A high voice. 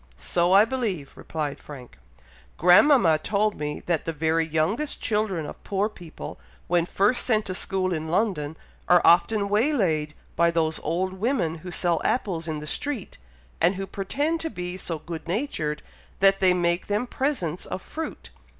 No: medium, 180 Hz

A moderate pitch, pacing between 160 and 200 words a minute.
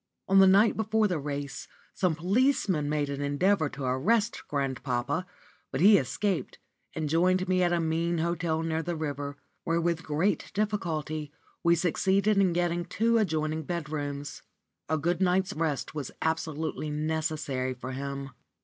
No: medium, 160 Hz; average, 150 wpm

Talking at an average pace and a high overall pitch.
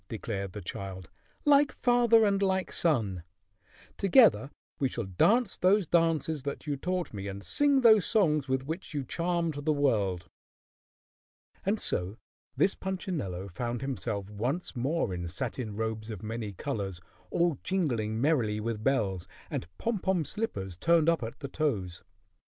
No: average, 150 wpm; low, 135 Hz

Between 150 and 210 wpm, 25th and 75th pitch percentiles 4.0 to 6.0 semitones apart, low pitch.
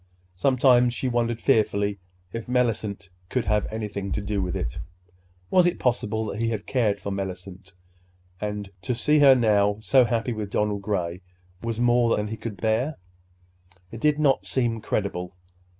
No: average, 165 wpm; average, 3.2 semitones; low, 110 Hz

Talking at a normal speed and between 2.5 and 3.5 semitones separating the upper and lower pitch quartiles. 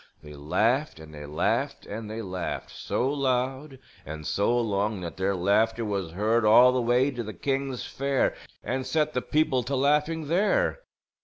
No: average, 170 wpm; wide, 5.4 semitones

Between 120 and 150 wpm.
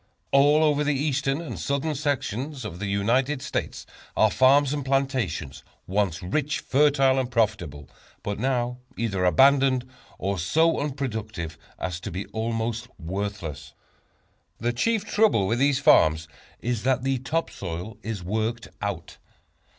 Yes: average, 140 wpm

